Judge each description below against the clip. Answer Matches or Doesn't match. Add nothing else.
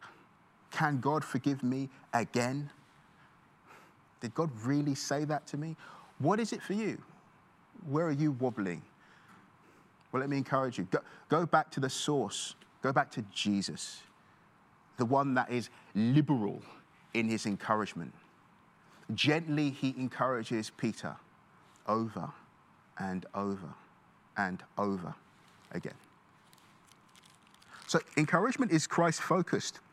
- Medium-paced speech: Doesn't match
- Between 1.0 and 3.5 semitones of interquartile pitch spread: Doesn't match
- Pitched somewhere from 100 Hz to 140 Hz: Matches